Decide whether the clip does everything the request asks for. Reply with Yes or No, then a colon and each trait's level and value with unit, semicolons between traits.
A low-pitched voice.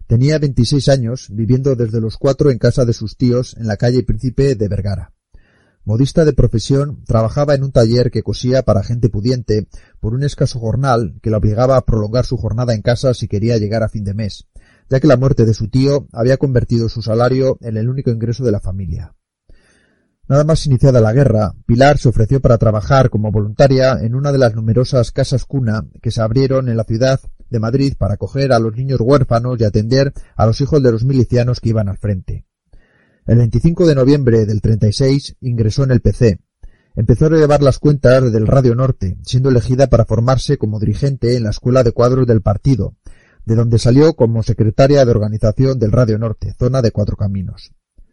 Yes: low, 120 Hz